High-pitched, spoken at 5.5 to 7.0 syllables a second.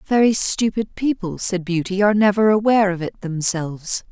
No: high, 195 Hz; 5.3 syllables/s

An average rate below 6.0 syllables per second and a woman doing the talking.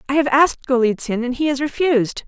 No: 6.5 syllables/s; female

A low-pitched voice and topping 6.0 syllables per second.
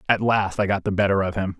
Yes: low, 100 Hz; 6.4 syllables/s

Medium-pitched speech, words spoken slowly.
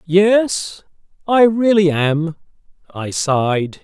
Yes: medium, 180 Hz; slow, 95 wpm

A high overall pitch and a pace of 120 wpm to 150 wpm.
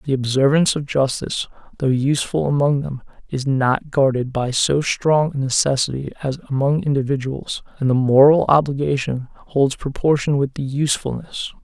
No: medium, 140 Hz; average, 145 wpm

